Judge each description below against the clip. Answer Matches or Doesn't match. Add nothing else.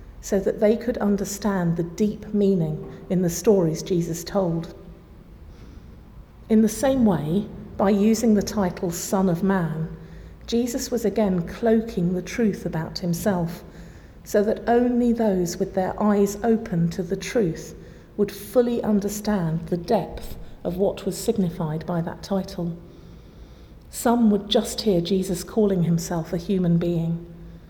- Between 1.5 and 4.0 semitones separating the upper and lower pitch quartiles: Matches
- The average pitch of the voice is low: Doesn't match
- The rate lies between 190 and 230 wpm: Doesn't match